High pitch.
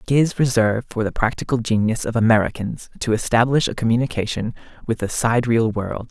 No: low, 115 Hz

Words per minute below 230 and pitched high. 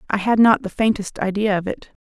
No: fast, 235 wpm; high, 205 Hz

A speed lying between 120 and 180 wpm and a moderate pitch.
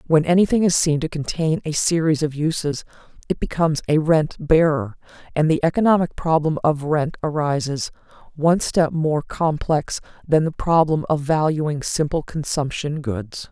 Yes: average, 150 wpm; medium, 155 Hz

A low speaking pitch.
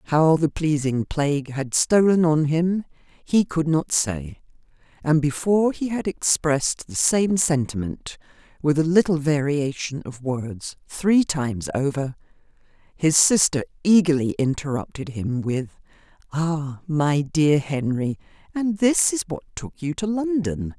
No: medium, 155 Hz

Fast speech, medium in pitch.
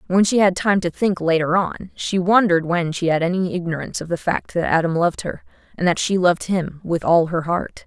Yes: fast, 235 wpm; medium, 175 Hz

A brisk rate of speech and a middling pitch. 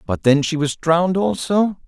No: average, 190 wpm; medium, 170 Hz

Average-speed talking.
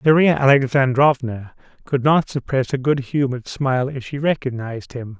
Yes: average, 150 wpm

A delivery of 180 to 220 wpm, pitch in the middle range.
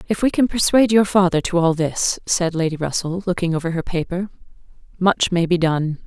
Yes: average, 200 wpm; medium, 175 Hz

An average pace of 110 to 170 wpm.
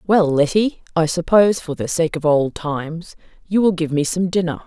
No: fast, 205 wpm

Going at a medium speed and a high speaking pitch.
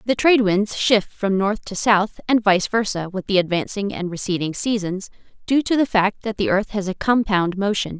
No: fast, 210 wpm; high, 200 Hz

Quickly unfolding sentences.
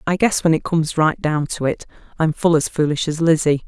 Yes: fast, 245 wpm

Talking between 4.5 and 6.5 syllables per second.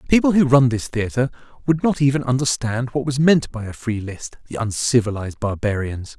Yes: 5.7 syllables/s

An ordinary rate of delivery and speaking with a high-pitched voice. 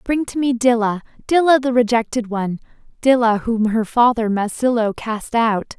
Yes: average, 155 wpm; high, 235 Hz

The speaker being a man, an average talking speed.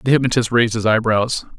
Yes: male; average, 190 wpm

